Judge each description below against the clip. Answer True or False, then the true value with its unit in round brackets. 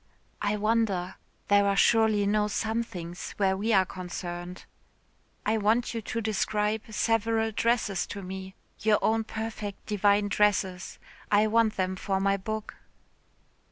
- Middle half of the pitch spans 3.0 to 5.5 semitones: False (2.4 semitones)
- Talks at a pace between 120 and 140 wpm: True (135 wpm)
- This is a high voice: True (210 Hz)